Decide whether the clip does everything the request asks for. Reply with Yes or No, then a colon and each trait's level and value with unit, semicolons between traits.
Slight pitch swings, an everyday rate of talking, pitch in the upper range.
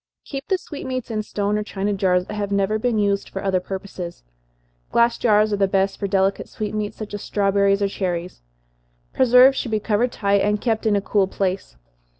Yes: narrow, 1.8 semitones; average, 195 wpm; high, 205 Hz